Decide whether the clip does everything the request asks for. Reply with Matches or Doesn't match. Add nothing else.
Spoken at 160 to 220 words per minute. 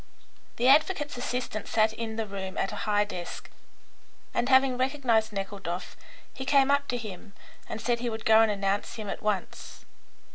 Matches